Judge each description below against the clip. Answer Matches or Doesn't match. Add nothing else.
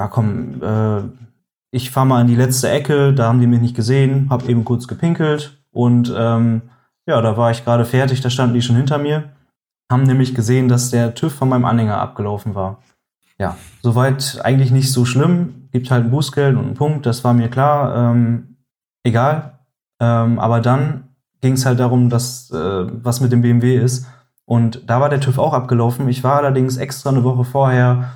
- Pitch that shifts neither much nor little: Doesn't match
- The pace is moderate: Doesn't match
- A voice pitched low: Matches